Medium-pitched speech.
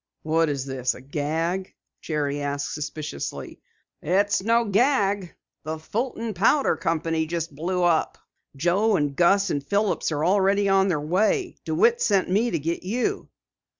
Yes: medium, 175 Hz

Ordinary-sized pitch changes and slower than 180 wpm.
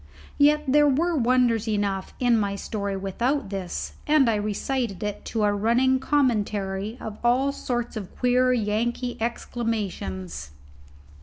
Yes: average, 3.9 semitones; slow, 135 wpm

